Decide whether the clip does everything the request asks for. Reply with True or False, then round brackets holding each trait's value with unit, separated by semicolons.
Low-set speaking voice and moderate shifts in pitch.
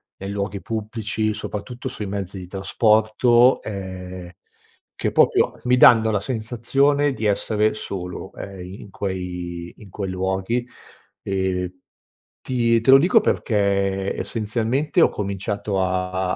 True (100 Hz; 3.4 semitones)